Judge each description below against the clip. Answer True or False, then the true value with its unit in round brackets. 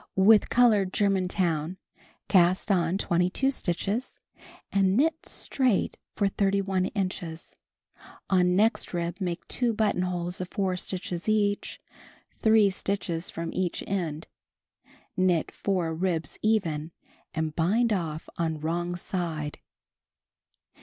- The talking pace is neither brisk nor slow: False (110 wpm)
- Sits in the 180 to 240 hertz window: True (185 Hz)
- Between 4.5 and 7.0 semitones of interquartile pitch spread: False (3.0 semitones)